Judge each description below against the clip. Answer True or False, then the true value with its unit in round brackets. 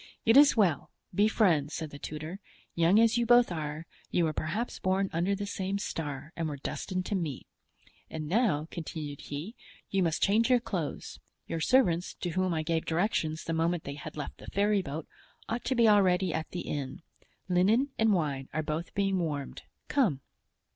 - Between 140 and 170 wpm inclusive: False (185 wpm)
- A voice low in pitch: False (175 Hz)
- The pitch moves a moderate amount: True (4.6 semitones)